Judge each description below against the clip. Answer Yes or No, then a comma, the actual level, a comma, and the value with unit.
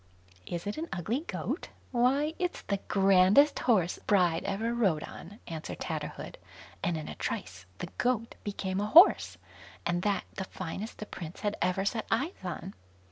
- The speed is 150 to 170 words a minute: Yes, average, 165 wpm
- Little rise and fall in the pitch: No, average, 4.8 semitones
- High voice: Yes, high, 200 Hz